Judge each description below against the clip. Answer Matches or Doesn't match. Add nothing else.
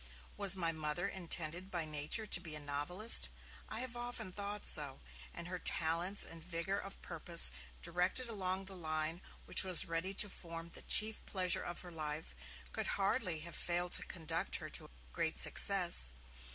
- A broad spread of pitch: Doesn't match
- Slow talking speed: Doesn't match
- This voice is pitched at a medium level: Matches